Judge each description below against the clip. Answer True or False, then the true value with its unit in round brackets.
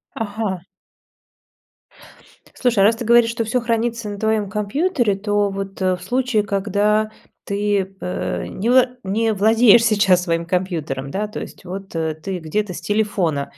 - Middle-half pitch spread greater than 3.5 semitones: False (2.9 semitones)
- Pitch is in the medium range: False (205 Hz)